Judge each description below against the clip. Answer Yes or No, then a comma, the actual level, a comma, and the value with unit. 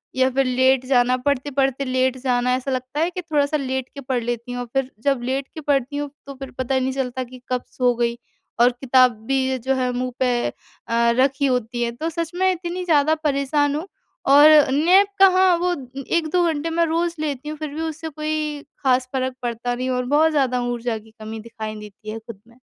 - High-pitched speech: Yes, very high, 265 Hz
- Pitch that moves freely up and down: No, average, 3.4 semitones